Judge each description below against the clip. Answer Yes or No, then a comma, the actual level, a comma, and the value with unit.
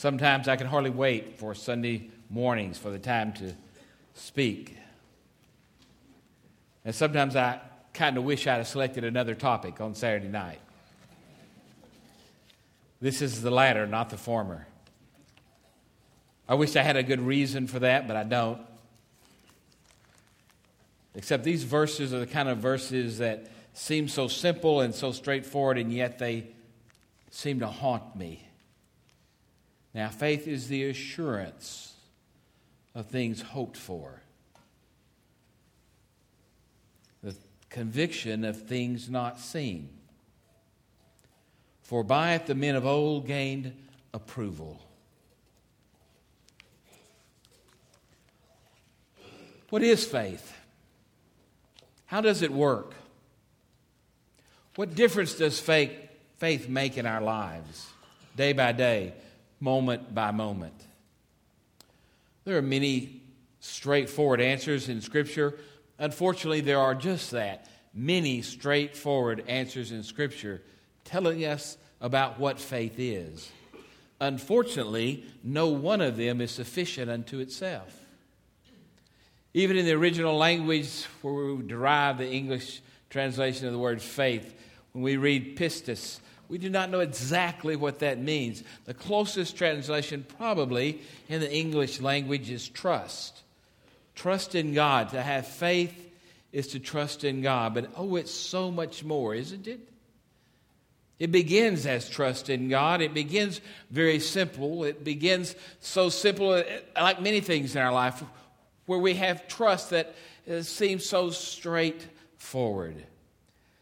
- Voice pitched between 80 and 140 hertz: Yes, low, 135 Hz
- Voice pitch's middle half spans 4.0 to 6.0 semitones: Yes, average, 4.8 semitones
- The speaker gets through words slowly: Yes, slow, 120 wpm